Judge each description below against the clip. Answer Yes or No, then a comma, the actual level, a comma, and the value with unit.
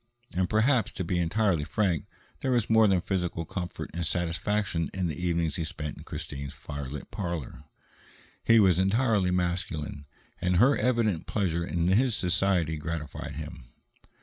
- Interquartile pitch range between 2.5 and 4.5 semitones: Yes, average, 3.8 semitones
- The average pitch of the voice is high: No, very low, 90 Hz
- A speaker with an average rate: Yes, average, 150 wpm